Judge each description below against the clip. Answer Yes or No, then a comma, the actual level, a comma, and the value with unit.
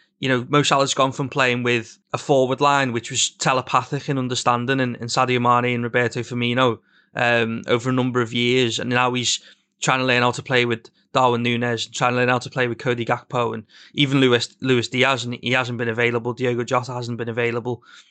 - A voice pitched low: Yes, low, 125 Hz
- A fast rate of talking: Yes, fast, 220 wpm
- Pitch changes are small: Yes, narrow, 1.3 semitones